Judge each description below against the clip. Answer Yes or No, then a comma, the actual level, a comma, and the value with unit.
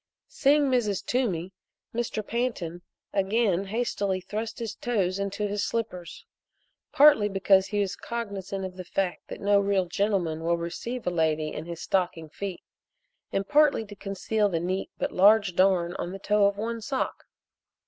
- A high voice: Yes, high, 200 Hz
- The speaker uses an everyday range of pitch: Yes, average, 3.3 semitones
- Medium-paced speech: Yes, average, 160 wpm